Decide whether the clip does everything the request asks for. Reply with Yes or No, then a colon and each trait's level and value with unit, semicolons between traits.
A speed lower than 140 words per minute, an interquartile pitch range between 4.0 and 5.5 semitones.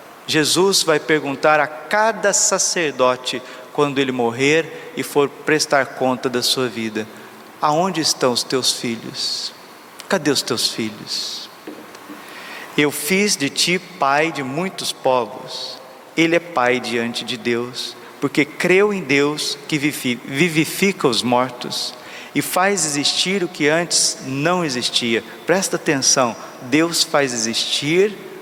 Yes: average, 125 wpm; average, 5.1 semitones